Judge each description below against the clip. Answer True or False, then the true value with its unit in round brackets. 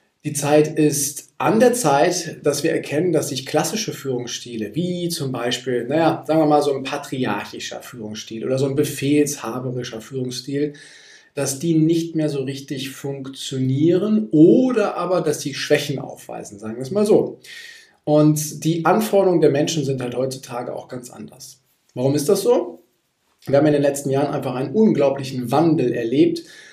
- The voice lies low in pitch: False (145 Hz)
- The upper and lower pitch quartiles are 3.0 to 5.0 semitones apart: True (3.5 semitones)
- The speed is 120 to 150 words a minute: False (165 wpm)